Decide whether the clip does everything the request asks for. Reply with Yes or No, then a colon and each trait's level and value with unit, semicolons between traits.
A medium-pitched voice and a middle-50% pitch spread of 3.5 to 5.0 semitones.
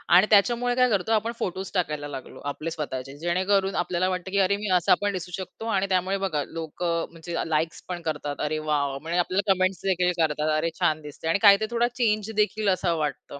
Yes: medium, 180 Hz; average, 4.1 semitones